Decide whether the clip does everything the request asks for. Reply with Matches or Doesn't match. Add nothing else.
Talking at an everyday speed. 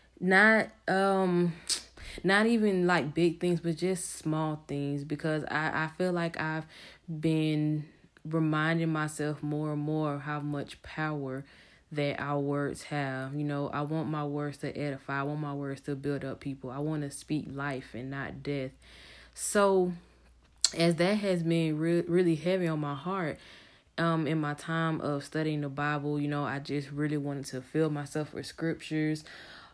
Matches